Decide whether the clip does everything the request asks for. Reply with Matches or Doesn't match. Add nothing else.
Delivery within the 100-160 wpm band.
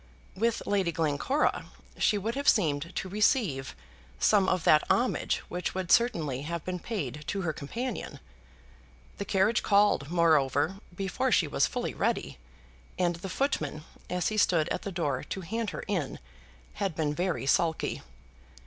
Matches